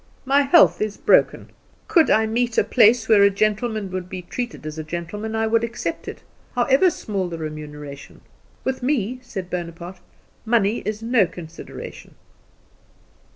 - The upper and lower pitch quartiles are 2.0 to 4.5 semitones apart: No, average, 5.3 semitones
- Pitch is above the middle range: Yes, high, 215 Hz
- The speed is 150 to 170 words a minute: Yes, average, 155 wpm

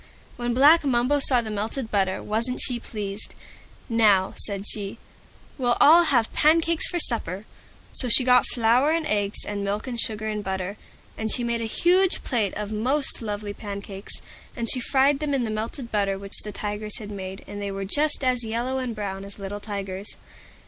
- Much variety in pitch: No, average, 3.9 semitones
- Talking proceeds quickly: No, average, 190 wpm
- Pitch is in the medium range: No, high, 220 Hz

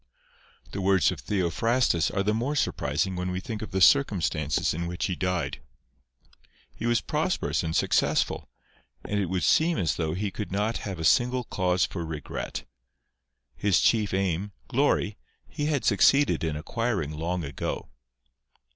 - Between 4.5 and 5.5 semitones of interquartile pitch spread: Yes, average, 5.0 semitones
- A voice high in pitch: No, very low, 95 Hz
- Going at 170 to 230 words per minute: No, average, 155 wpm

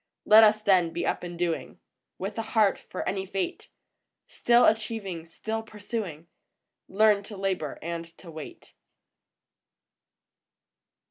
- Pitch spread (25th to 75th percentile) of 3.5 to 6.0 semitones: Yes, average, 3.9 semitones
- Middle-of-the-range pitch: No, high, 195 Hz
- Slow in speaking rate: Yes, slow, 125 wpm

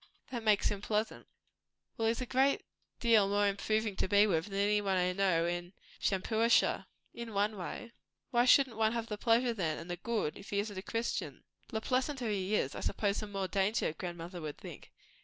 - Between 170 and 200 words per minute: Yes, average, 195 wpm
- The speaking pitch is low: No, high, 205 Hz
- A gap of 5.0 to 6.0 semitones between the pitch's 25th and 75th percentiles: No, average, 3.2 semitones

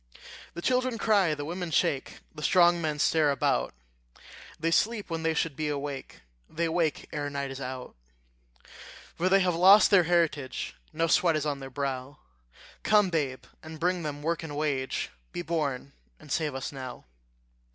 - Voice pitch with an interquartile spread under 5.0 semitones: Yes, average, 3.4 semitones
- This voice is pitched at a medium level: Yes, medium, 155 Hz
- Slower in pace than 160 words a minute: No, average, 170 wpm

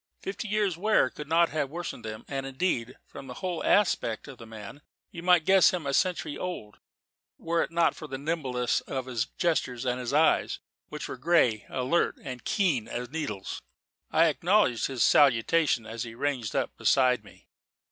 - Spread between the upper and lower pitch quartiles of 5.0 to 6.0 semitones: Yes, wide, 5.4 semitones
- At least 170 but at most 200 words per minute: Yes, average, 180 wpm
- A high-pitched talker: No, medium, 140 Hz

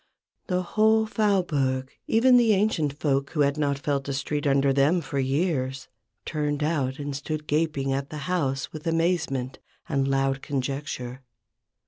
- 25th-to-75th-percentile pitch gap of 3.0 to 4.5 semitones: Yes, average, 3.3 semitones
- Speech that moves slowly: No, average, 150 wpm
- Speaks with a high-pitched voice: No, medium, 145 Hz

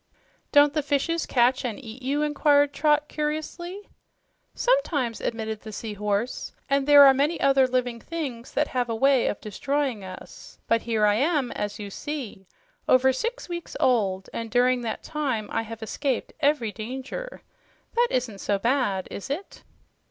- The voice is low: No, very high, 255 Hz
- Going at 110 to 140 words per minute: No, average, 165 wpm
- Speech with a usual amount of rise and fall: Yes, average, 4.7 semitones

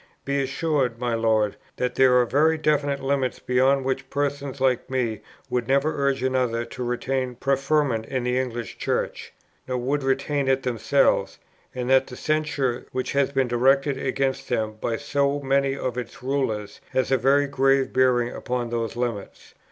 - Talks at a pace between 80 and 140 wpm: No, average, 165 wpm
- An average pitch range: No, narrow, 2.1 semitones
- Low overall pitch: Yes, low, 130 Hz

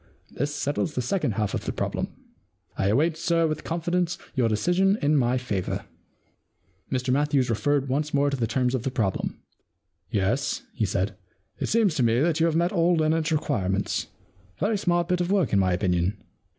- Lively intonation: Yes, wide, 6.6 semitones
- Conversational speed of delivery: Yes, average, 190 wpm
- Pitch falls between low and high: Yes, medium, 145 Hz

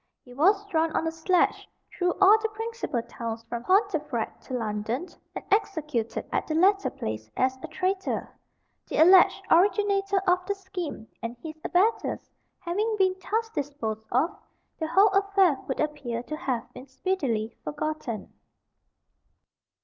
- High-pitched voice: Yes, very high, 320 Hz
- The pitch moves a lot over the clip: Yes, wide, 7.8 semitones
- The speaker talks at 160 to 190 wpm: No, average, 145 wpm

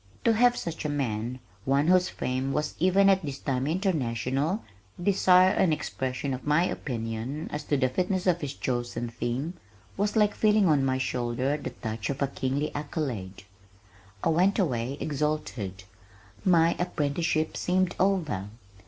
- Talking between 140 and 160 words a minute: Yes, average, 155 wpm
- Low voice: No, medium, 145 Hz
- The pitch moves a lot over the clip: Yes, wide, 5.8 semitones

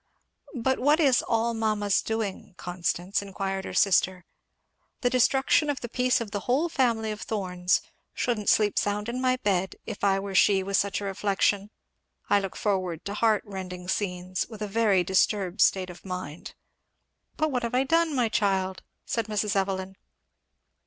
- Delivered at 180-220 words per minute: No, average, 170 wpm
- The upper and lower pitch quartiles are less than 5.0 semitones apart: Yes, average, 3.4 semitones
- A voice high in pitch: Yes, high, 205 Hz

